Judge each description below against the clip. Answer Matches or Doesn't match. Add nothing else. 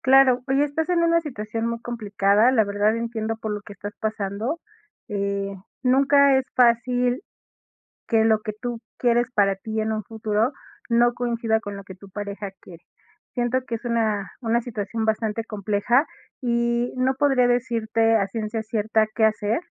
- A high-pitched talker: Matches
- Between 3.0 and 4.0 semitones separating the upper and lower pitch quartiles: Doesn't match